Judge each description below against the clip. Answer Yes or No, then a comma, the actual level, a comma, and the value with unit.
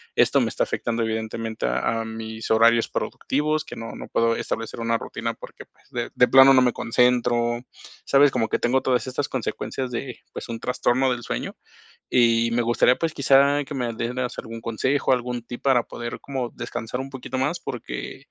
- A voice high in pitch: No, low, 120 Hz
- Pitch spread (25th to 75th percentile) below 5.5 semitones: Yes, narrow, 2.4 semitones